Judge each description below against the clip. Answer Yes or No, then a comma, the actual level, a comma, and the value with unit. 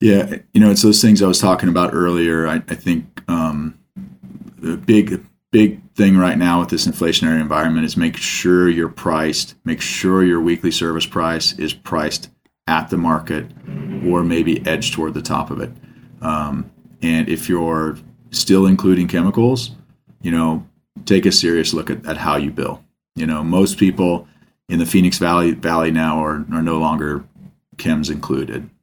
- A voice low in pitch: Yes, very low, 85 Hz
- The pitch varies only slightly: No, average, 3.0 semitones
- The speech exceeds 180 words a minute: No, average, 175 wpm